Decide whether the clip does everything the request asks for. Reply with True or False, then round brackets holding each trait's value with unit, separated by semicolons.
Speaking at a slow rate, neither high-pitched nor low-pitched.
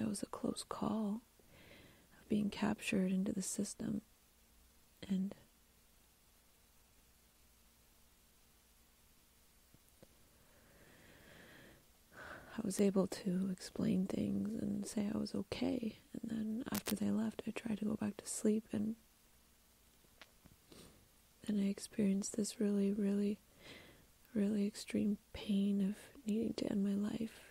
False (110 wpm; 205 Hz)